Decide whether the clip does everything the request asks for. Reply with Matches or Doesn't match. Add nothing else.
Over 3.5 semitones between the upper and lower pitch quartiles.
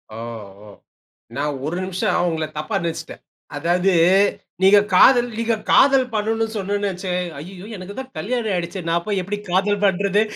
Doesn't match